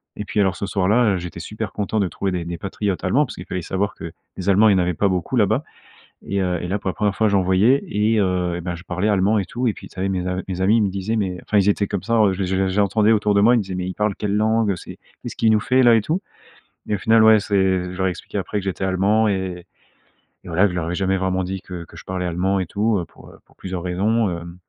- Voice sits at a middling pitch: No, very low, 95 Hz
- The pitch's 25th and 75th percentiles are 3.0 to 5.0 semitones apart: No, narrow, 2.5 semitones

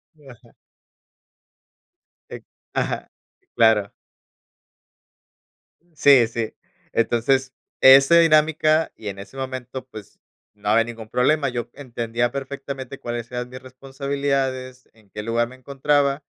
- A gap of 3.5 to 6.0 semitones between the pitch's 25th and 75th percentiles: No, average, 2.9 semitones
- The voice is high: No, low, 130 Hz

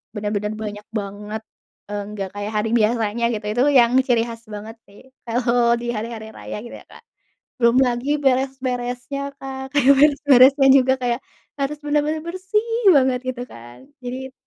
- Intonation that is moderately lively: Yes, average, 3.7 semitones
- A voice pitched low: No, high, 245 Hz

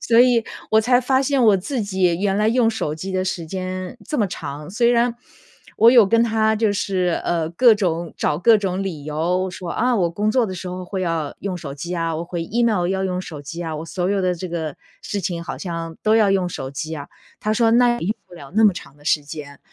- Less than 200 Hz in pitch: Yes, medium, 185 Hz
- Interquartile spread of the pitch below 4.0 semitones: No, average, 4.7 semitones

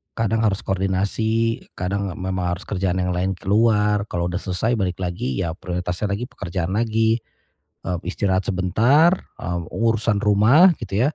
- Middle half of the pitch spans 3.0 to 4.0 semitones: Yes, average, 3.6 semitones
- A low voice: Yes, low, 100 Hz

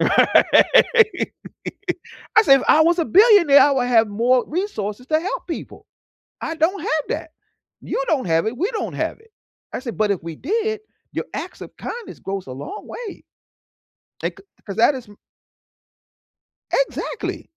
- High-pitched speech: Yes, very high, 305 Hz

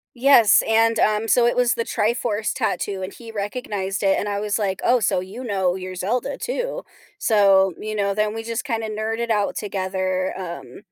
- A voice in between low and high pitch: No, high, 210 Hz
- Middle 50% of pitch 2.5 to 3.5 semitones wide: Yes, average, 3.0 semitones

